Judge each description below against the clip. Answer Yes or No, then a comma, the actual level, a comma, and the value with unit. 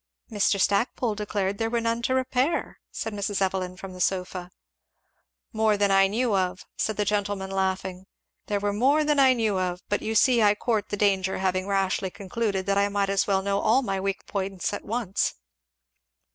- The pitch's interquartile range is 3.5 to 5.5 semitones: No, narrow, 2.4 semitones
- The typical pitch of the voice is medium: No, high, 200 Hz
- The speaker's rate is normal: Yes, average, 190 wpm